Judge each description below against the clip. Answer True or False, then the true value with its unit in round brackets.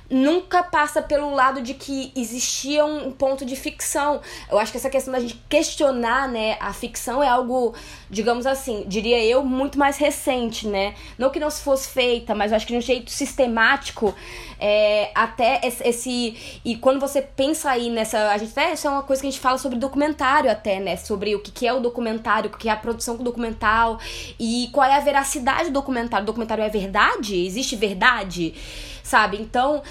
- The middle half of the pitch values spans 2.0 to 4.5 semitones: True (3.6 semitones)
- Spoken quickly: True (195 wpm)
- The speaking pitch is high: True (250 Hz)